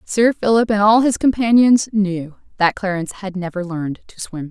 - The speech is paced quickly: No, average, 185 wpm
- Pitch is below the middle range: No, high, 200 Hz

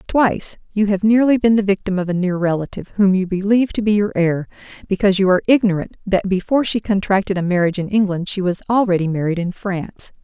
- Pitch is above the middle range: Yes, high, 195 Hz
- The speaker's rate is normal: No, fast, 210 wpm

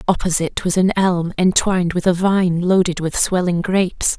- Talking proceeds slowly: No, average, 170 wpm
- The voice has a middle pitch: Yes, medium, 180 Hz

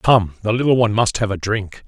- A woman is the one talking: No, male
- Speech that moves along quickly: Yes, fast, 255 wpm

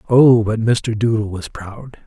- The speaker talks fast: No, average, 175 wpm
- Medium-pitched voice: No, low, 110 Hz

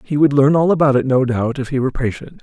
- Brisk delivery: Yes, fast, 295 wpm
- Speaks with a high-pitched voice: No, low, 135 Hz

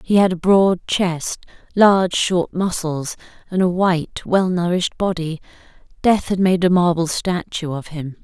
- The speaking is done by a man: No, female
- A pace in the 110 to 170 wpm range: Yes, average, 160 wpm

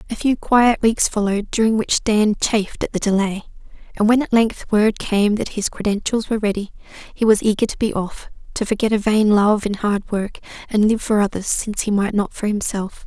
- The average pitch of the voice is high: Yes, high, 210 Hz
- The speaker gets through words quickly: Yes, fast, 215 wpm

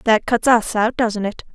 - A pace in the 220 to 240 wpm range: Yes, fast, 235 wpm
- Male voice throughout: No, female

